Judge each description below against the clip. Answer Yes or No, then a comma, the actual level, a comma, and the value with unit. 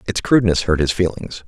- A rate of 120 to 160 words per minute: No, fast, 205 wpm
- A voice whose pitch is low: Yes, very low, 90 Hz